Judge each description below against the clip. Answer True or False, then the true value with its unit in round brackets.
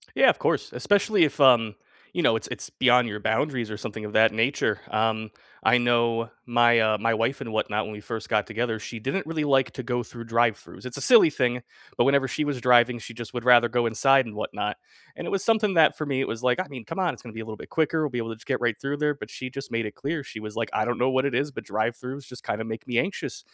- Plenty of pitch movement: False (3.5 semitones)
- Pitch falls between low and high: False (120 Hz)